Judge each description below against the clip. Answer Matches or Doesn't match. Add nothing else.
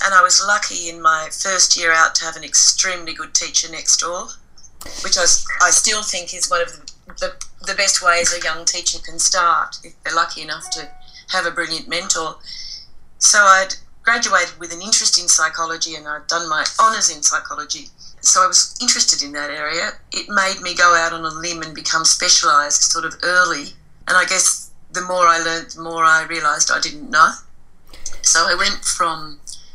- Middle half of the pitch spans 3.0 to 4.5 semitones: Doesn't match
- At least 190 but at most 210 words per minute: Matches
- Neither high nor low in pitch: Matches